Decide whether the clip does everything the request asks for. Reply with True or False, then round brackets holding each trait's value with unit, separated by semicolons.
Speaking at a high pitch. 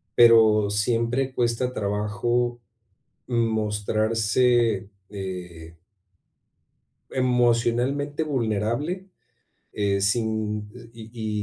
False (115 Hz)